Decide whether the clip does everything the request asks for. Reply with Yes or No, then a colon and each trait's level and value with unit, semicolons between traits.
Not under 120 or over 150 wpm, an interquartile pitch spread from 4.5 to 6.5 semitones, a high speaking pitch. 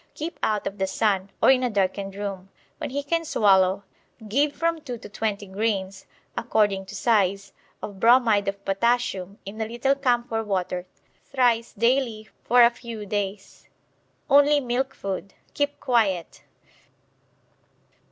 No: average, 140 wpm; average, 4.0 semitones; high, 215 Hz